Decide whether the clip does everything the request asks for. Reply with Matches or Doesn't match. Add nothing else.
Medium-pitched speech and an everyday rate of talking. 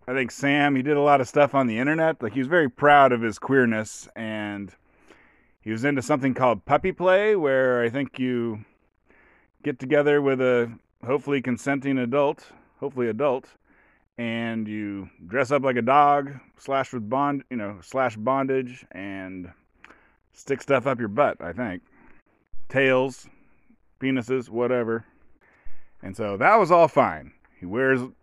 Doesn't match